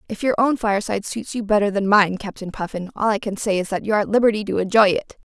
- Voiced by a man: No, female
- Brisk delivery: Yes, fast, 260 wpm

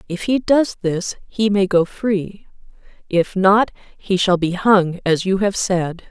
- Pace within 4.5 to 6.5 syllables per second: No, 3.7 syllables/s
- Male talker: No, female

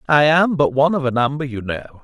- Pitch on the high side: No, medium, 140 Hz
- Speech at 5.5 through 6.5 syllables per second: Yes, 5.9 syllables/s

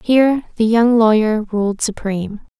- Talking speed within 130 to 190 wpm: Yes, average, 140 wpm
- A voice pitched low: No, high, 220 Hz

